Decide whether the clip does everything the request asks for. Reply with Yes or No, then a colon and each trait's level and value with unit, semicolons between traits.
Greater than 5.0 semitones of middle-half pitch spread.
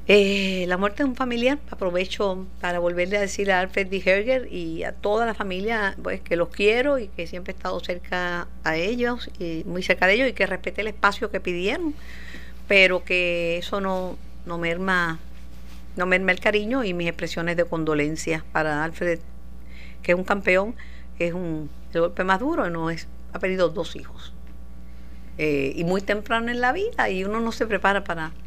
No: average, 3.2 semitones